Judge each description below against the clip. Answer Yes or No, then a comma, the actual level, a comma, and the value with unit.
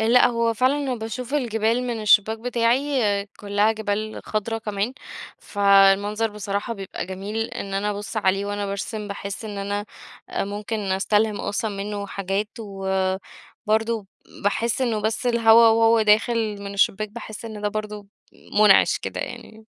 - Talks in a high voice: Yes, high, 210 Hz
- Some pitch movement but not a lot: No, narrow, 2.0 semitones